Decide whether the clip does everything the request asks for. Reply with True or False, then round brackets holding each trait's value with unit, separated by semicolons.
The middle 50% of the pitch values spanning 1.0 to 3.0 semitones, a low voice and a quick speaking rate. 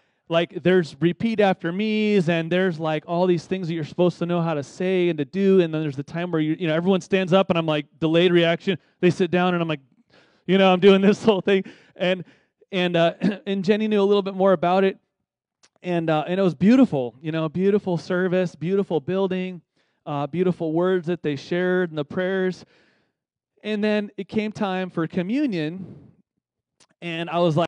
False (2.6 semitones; 180 Hz; 210 wpm)